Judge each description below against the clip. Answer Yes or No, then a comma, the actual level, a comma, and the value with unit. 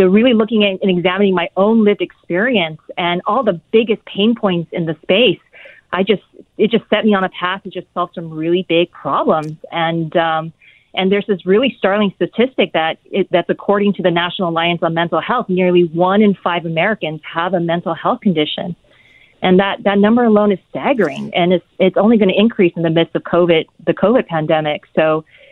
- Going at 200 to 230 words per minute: Yes, fast, 205 wpm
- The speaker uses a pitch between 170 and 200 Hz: Yes, medium, 185 Hz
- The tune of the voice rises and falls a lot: No, average, 3.4 semitones